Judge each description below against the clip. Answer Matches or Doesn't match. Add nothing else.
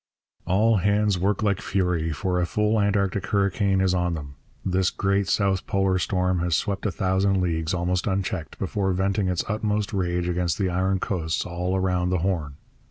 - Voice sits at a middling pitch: Doesn't match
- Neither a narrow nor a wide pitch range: Doesn't match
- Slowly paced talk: Doesn't match